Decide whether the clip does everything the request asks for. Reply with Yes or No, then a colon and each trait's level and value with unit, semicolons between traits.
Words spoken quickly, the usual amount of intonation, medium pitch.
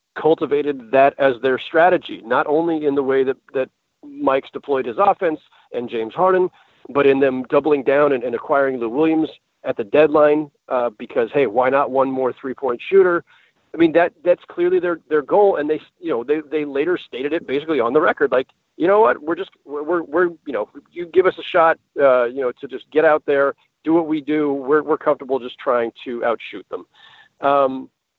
Yes: fast, 215 wpm; average, 3.3 semitones; medium, 145 Hz